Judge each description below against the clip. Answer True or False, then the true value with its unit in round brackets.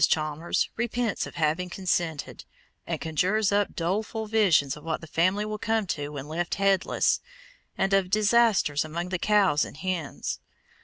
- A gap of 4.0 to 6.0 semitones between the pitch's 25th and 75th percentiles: True (4.9 semitones)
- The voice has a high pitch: False (180 Hz)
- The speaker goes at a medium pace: True (155 wpm)